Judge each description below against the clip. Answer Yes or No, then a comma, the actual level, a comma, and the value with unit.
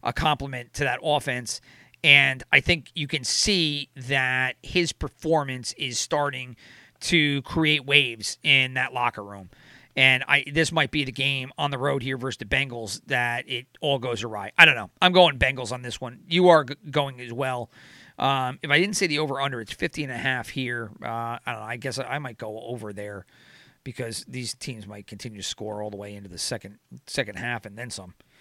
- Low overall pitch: Yes, low, 130 Hz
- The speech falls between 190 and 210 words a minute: Yes, average, 200 wpm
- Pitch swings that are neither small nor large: Yes, average, 3.4 semitones